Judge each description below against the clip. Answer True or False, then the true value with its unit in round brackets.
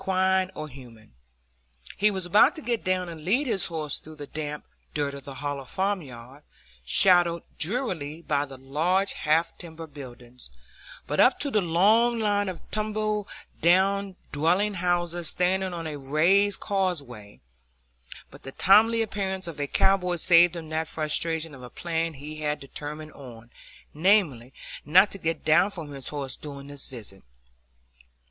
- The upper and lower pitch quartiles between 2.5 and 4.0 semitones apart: False (4.8 semitones)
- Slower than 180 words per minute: True (145 wpm)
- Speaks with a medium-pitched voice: True (165 Hz)